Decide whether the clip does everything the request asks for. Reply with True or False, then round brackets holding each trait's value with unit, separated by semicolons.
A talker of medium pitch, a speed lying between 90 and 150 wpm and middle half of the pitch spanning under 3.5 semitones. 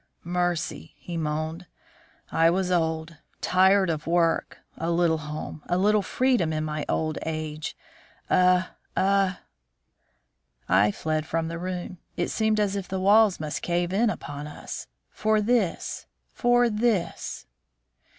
False (175 Hz; 140 wpm; 3.8 semitones)